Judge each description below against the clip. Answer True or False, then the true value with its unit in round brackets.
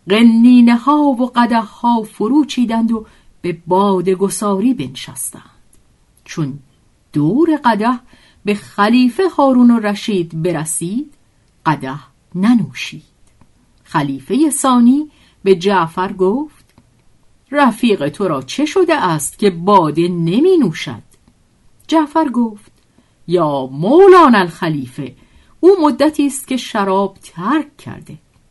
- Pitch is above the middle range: True (220 Hz)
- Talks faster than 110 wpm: False (105 wpm)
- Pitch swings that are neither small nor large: False (7.1 semitones)